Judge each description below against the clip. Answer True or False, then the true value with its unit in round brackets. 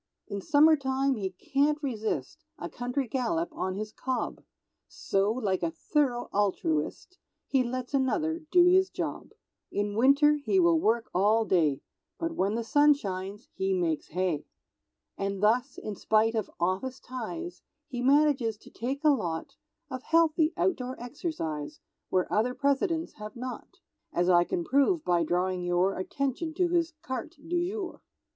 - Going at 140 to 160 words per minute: True (150 wpm)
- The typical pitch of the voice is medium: False (245 Hz)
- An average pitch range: False (7.3 semitones)